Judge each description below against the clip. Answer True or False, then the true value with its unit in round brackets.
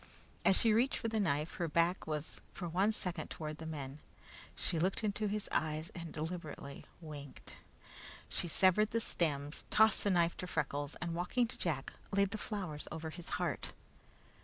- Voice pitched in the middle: True (170 Hz)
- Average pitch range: True (4.6 semitones)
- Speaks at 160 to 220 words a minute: True (175 wpm)